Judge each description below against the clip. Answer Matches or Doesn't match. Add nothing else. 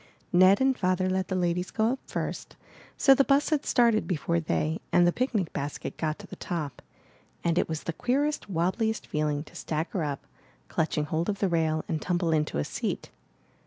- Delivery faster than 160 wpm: Matches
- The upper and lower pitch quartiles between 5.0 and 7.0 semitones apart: Matches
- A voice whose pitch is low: Doesn't match